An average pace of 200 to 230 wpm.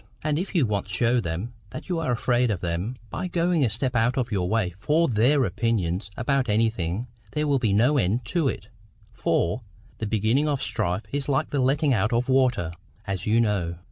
Yes: fast, 205 wpm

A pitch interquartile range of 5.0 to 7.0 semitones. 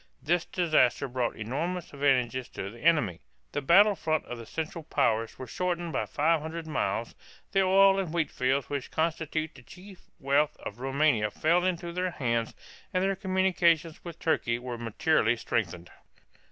Yes: wide, 5.5 semitones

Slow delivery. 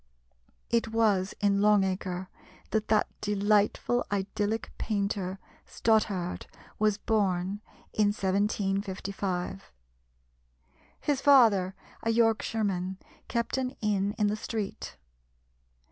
Yes: slow, 95 wpm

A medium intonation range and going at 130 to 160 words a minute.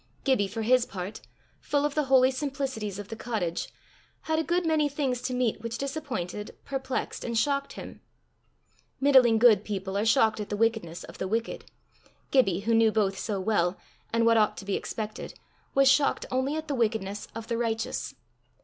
No: average, 4.3 semitones; average, 185 wpm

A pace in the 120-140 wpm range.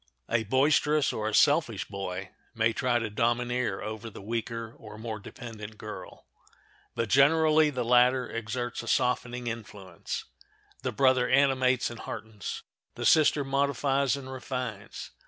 Yes: slow, 135 wpm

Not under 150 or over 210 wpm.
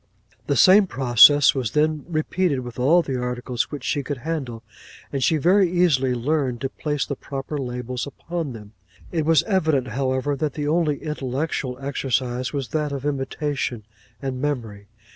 Yes: average, 160 wpm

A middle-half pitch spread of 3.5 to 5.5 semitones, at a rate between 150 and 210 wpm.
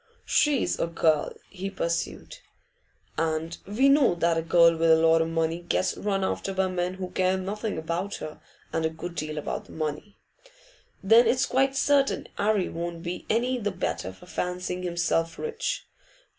Yes: average, 3.8 semitones; average, 170 wpm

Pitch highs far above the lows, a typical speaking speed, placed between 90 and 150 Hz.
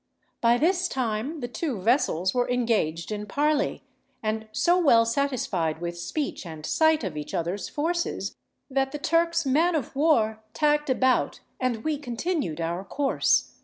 No: wide, 6.3 semitones; average, 155 wpm; very high, 250 Hz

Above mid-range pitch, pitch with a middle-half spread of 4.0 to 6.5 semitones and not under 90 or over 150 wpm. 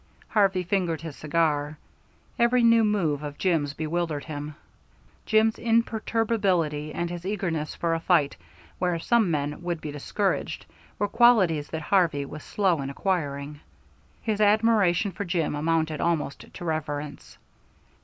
No: medium, 170 Hz; average, 5.1 semitones; slow, 135 wpm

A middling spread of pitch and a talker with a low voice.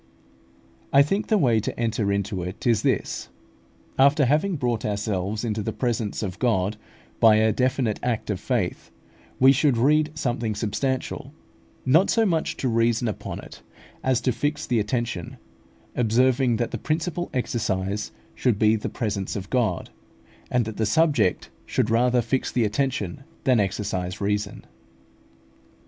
Yes: average, 3.9 semitones; low, 115 Hz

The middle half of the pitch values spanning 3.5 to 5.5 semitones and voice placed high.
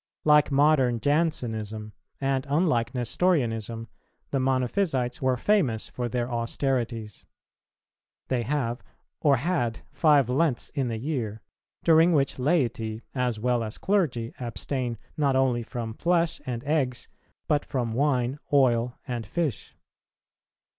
No: average, 3.8 semitones; low, 125 Hz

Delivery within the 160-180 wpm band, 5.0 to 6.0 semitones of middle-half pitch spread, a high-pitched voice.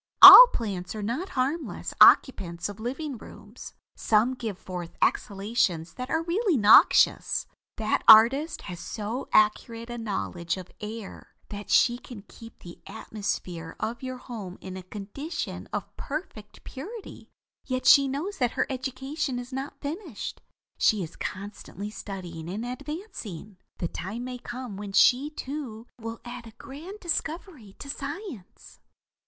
No: average, 140 wpm; average, 5.3 semitones; high, 235 Hz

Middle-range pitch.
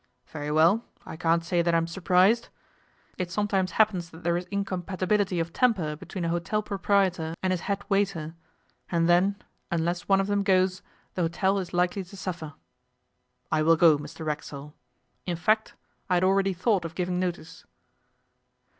Yes: medium, 180 Hz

